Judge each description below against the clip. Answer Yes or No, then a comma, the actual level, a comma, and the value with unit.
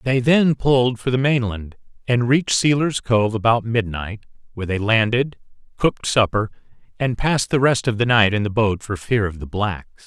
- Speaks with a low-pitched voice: Yes, low, 115 Hz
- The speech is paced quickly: No, average, 190 wpm